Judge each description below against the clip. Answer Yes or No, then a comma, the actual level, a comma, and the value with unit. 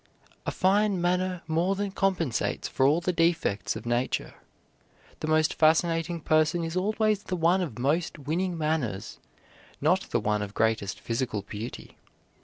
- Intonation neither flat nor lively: No, wide, 6.2 semitones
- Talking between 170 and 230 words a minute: No, average, 150 wpm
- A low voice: No, medium, 165 Hz